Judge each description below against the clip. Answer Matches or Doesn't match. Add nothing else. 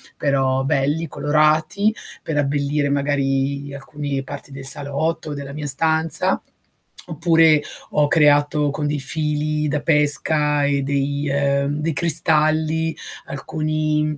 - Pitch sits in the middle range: Matches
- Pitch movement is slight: Matches